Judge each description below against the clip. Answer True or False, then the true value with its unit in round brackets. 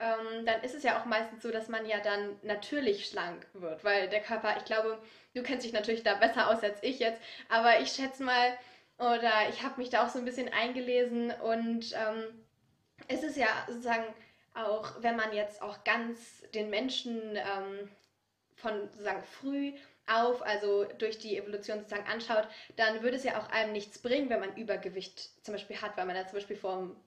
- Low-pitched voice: False (220 Hz)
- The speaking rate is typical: False (195 wpm)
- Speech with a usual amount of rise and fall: False (2.1 semitones)